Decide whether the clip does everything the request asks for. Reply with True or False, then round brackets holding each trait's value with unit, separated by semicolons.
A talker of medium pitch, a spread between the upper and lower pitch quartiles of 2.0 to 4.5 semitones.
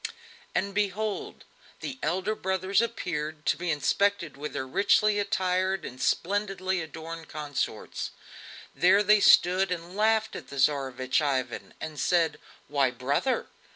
False (180 Hz; 5.1 semitones)